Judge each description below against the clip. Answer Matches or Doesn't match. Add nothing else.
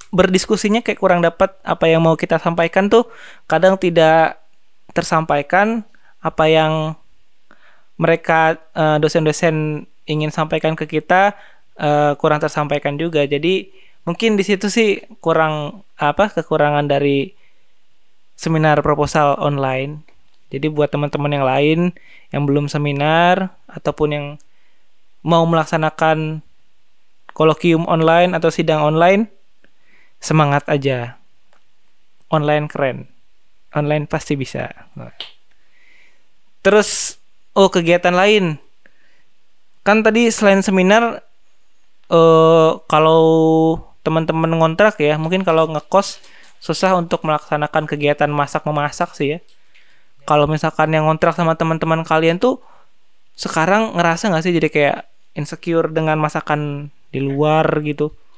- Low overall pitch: Doesn't match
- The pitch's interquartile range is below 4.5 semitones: Matches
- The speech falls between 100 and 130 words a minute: Matches